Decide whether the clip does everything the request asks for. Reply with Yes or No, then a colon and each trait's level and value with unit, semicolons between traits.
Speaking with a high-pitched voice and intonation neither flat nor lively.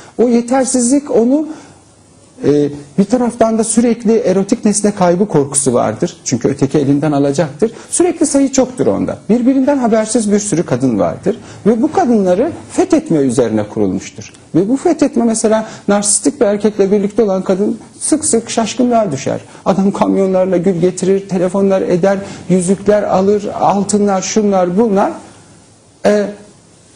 Yes: high, 205 Hz; average, 4.5 semitones